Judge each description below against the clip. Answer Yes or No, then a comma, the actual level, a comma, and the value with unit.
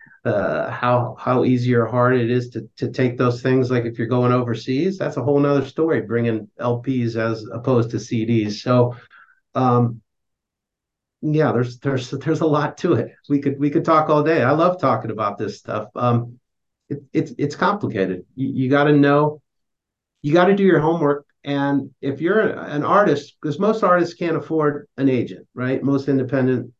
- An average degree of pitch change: Yes, average, 3.6 semitones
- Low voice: Yes, low, 130 Hz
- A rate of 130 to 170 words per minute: No, average, 185 wpm